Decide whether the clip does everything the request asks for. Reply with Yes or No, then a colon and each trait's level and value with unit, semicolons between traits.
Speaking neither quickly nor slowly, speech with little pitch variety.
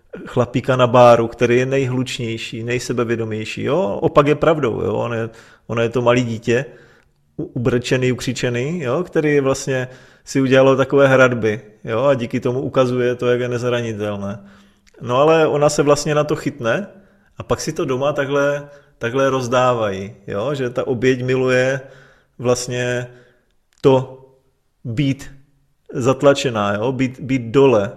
Yes: average, 140 wpm; narrow, 2.3 semitones